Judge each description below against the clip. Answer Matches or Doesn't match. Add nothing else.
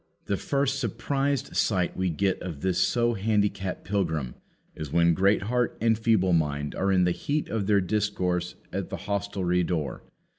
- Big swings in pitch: Doesn't match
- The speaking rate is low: Doesn't match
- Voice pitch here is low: Matches